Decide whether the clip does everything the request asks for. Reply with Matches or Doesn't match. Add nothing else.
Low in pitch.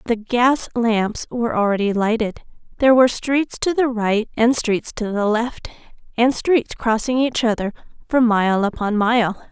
Doesn't match